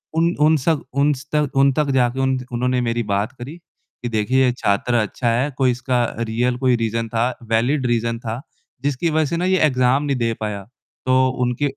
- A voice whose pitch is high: No, low, 125 Hz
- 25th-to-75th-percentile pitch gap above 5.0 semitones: No, average, 3.1 semitones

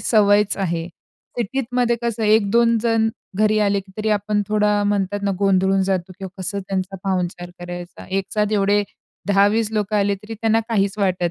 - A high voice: Yes, high, 205 Hz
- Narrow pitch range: Yes, narrow, 1.9 semitones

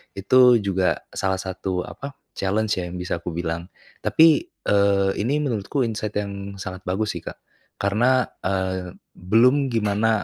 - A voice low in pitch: Yes, low, 100 Hz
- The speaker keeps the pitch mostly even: No, average, 3.1 semitones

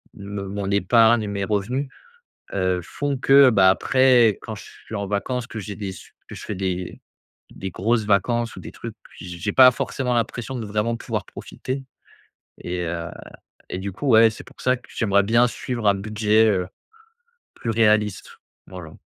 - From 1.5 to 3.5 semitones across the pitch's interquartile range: Yes, average, 3.2 semitones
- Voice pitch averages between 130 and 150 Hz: No, low, 105 Hz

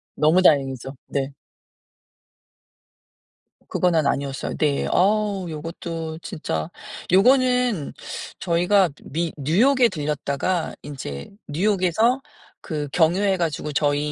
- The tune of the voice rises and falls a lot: No, average, 4.8 semitones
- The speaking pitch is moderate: Yes, medium, 165 Hz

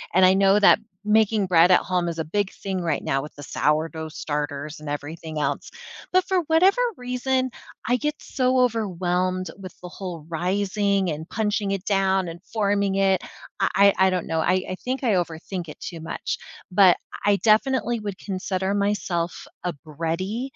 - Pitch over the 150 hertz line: Yes, high, 190 Hz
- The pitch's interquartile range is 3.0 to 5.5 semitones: Yes, average, 3.8 semitones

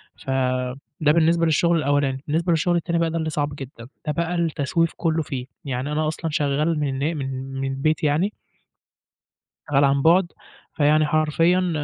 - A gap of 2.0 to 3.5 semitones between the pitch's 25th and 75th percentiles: Yes, average, 3.2 semitones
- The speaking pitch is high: No, medium, 150 Hz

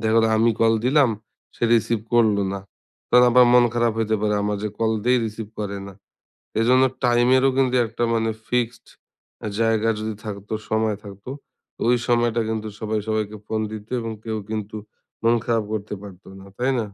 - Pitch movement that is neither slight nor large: No, narrow, 1.8 semitones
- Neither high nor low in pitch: No, low, 110 Hz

